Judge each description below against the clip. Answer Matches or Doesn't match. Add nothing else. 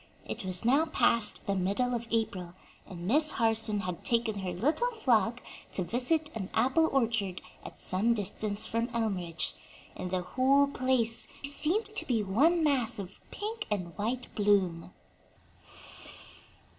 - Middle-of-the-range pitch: Doesn't match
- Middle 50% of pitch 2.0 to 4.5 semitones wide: Doesn't match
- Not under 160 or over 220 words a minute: Doesn't match